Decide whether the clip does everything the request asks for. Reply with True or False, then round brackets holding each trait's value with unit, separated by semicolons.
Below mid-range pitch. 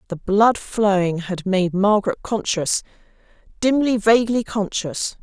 False (205 Hz)